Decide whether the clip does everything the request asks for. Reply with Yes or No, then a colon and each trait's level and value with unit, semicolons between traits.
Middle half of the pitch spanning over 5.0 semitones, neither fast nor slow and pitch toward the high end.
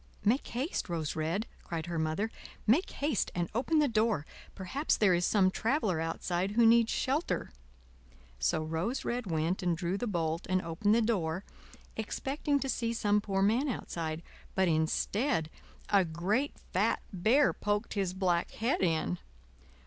Yes: wide, 5.6 semitones; average, 155 wpm; high, 195 Hz